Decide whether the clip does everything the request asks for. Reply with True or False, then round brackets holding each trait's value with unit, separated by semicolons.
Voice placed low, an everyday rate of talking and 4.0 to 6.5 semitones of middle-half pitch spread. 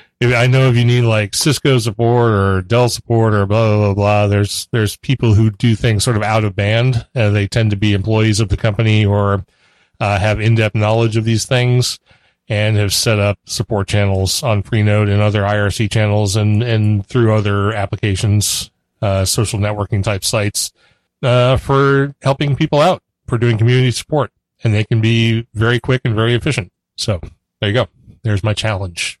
False (110 Hz; 185 wpm; 2.5 semitones)